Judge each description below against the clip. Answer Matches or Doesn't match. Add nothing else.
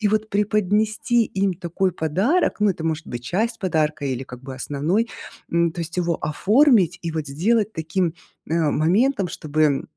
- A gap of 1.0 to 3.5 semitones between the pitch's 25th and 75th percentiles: Doesn't match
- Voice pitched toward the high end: Doesn't match